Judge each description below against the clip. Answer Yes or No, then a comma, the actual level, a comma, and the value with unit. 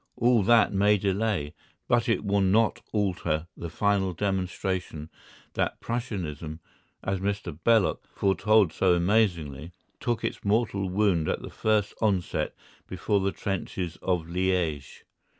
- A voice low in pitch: Yes, very low, 95 Hz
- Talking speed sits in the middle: No, slow, 130 wpm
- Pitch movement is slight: No, average, 3.3 semitones